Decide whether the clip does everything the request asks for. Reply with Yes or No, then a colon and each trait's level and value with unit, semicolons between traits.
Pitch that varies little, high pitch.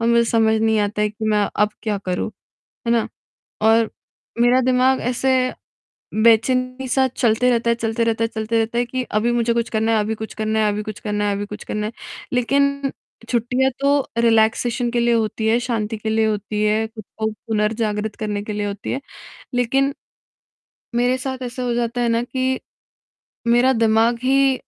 Yes: narrow, 2.3 semitones; high, 230 Hz